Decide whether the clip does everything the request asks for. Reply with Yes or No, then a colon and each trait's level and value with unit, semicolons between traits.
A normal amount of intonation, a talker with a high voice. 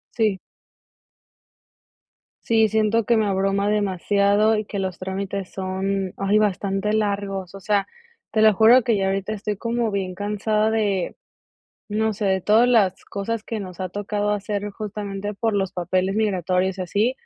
No: narrow, 1.9 semitones; high, 205 Hz